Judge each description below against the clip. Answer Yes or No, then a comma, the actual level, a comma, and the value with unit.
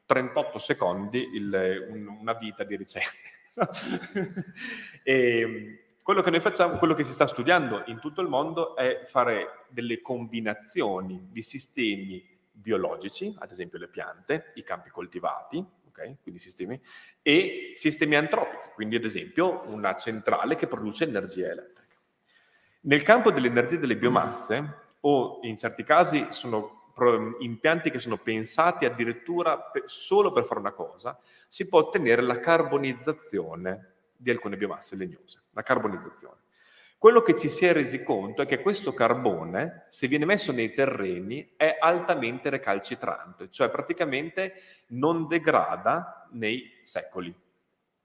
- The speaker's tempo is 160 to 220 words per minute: No, average, 135 wpm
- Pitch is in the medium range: No, low, 130 Hz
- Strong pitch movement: Yes, wide, 6.9 semitones